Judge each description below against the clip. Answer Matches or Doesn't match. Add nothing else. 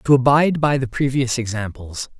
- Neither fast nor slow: Matches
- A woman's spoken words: Doesn't match